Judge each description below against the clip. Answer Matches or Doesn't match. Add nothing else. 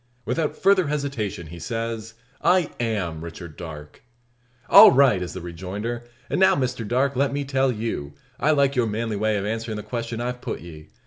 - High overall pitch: Doesn't match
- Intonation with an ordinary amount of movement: Doesn't match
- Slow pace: Doesn't match